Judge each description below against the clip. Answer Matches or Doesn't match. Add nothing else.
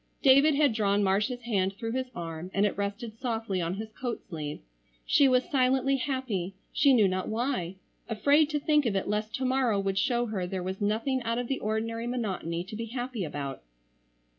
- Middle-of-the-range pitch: Doesn't match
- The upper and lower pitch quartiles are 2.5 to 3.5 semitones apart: Doesn't match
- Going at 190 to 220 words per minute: Matches